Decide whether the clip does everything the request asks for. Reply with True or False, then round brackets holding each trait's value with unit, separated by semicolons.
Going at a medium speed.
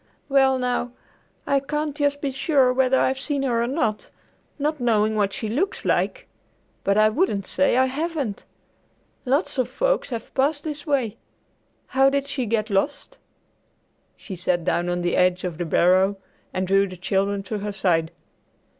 True (170 wpm)